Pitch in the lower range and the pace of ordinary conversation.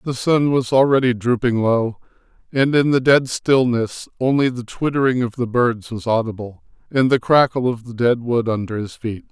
Yes: low, 120 Hz; average, 185 wpm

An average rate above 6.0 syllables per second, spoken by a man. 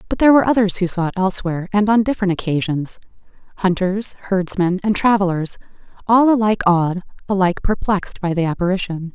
No: 6.5 syllables/s; female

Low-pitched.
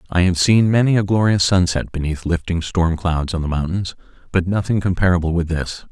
Yes: very low, 90 Hz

